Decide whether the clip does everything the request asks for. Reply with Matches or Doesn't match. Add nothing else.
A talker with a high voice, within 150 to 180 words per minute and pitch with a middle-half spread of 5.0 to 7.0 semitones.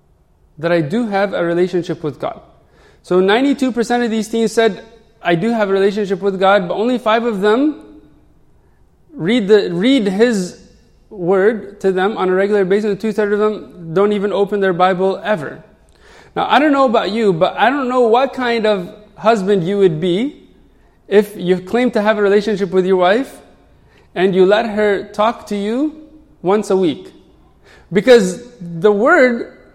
Doesn't match